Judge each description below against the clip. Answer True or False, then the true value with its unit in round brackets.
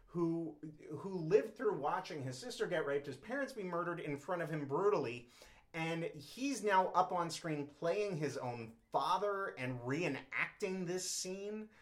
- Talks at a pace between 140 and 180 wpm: True (160 wpm)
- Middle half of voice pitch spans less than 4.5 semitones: False (5.0 semitones)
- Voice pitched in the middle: True (170 Hz)